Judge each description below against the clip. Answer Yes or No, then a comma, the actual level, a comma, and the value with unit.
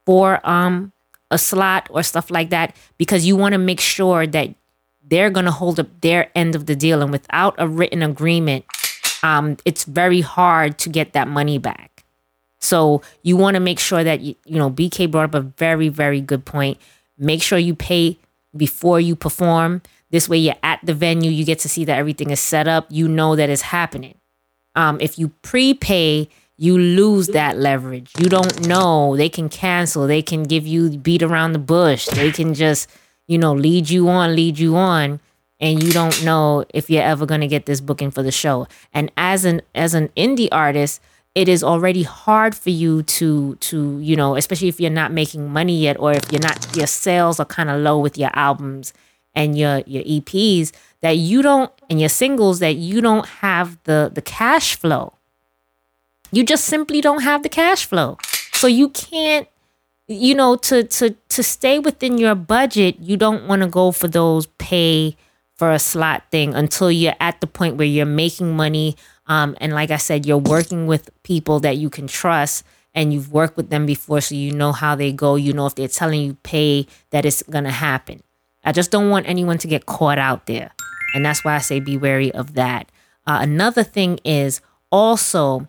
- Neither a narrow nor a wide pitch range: Yes, average, 3.4 semitones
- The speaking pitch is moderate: Yes, medium, 160 Hz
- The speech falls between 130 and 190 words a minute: No, average, 200 wpm